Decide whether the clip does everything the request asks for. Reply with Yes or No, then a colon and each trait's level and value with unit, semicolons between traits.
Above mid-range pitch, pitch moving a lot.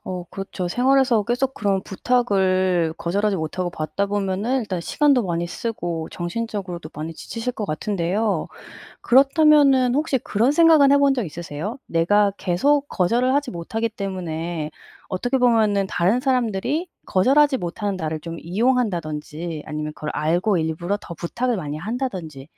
Yes: high, 200 Hz; wide, 6.4 semitones